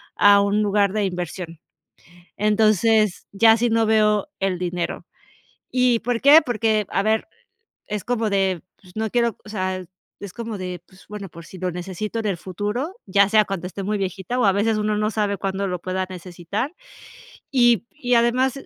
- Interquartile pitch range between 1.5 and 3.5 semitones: Yes, average, 3.1 semitones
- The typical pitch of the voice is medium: No, high, 210 Hz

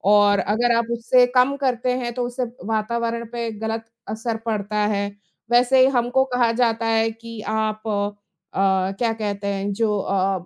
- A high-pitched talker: Yes, high, 225 Hz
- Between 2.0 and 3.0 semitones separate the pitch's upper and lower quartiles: Yes, average, 2.7 semitones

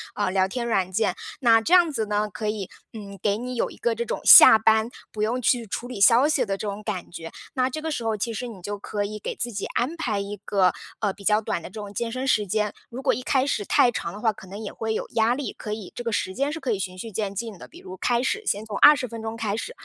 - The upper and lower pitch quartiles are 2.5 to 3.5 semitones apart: Yes, average, 3.1 semitones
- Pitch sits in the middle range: No, high, 220 Hz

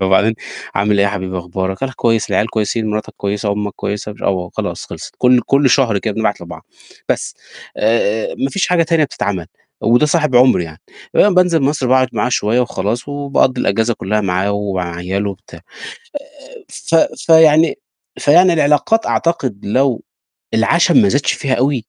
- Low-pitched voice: Yes, low, 115 Hz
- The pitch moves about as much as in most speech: No, wide, 6.0 semitones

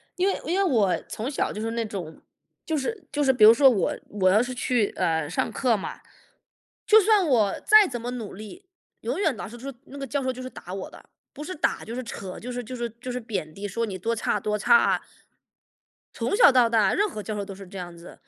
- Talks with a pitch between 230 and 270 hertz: Yes, high, 235 Hz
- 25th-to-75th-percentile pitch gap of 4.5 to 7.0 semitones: Yes, average, 5.0 semitones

